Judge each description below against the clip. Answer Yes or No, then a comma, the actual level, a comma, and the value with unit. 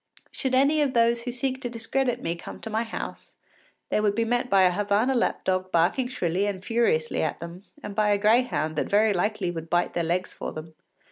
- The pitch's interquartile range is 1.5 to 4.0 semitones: No, average, 5.2 semitones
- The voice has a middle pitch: No, high, 210 Hz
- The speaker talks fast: Yes, fast, 220 wpm